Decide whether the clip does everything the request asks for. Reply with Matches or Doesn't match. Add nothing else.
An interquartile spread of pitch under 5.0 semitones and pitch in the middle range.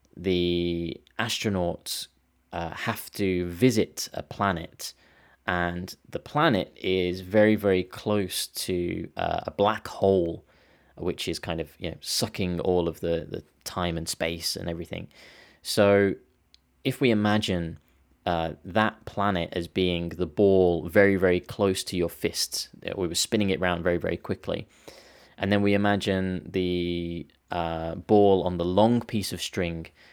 Doesn't match